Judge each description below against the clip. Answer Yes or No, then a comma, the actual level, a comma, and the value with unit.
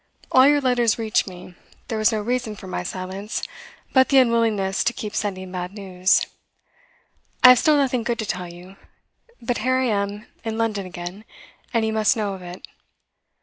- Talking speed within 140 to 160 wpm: No, average, 185 wpm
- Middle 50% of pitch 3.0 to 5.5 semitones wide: Yes, average, 3.9 semitones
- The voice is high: Yes, high, 215 Hz